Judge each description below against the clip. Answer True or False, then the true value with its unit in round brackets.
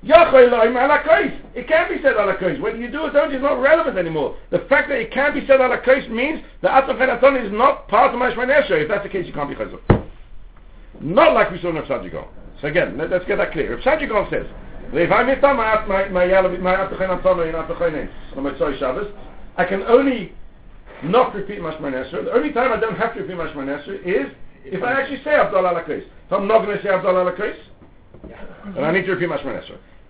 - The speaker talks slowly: False (195 wpm)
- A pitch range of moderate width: False (6.5 semitones)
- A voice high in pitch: True (225 Hz)